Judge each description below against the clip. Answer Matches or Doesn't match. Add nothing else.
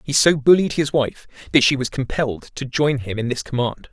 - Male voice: Matches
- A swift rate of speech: Matches